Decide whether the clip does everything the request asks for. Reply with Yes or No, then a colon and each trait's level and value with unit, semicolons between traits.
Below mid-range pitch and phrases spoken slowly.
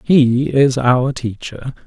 Yes: low, 130 Hz; slow, 130 wpm